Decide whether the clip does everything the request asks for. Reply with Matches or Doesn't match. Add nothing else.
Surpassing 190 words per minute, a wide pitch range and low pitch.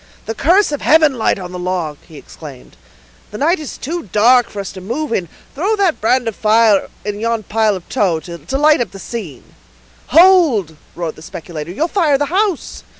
Doesn't match